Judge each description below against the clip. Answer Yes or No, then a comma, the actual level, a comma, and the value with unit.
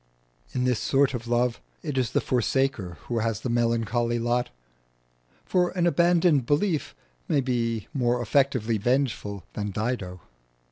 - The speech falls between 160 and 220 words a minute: No, average, 140 wpm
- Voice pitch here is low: Yes, low, 120 Hz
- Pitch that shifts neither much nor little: Yes, average, 3.0 semitones